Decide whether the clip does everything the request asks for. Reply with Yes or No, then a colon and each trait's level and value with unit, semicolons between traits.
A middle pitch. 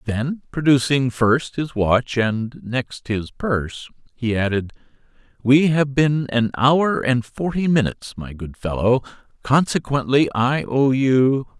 No: low, 125 Hz